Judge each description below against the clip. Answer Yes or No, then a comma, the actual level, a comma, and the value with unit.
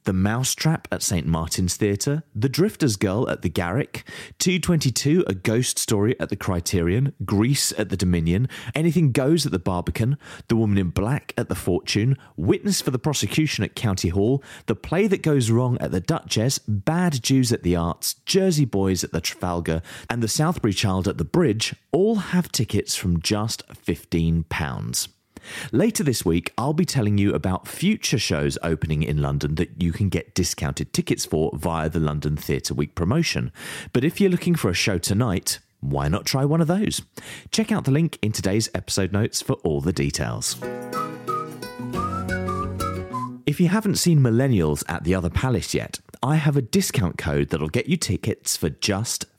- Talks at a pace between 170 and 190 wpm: Yes, average, 180 wpm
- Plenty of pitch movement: Yes, wide, 7.9 semitones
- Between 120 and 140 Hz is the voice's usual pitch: No, low, 105 Hz